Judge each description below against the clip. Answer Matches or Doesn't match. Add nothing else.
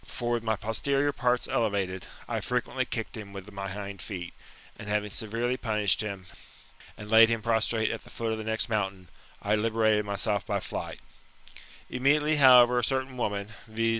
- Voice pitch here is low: Matches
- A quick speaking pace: Doesn't match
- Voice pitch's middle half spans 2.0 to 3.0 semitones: Matches